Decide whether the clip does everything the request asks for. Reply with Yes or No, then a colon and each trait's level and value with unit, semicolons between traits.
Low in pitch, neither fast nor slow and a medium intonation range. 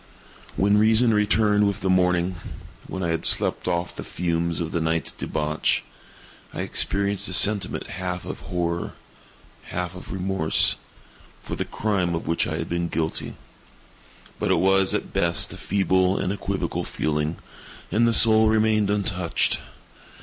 Yes: very low, 90 Hz; average, 145 wpm; average, 3.0 semitones